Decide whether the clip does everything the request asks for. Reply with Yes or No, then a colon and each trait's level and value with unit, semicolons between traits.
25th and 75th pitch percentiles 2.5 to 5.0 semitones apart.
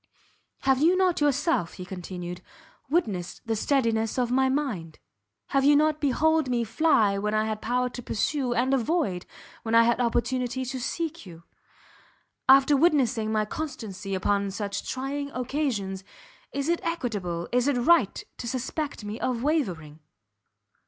No: wide, 5.6 semitones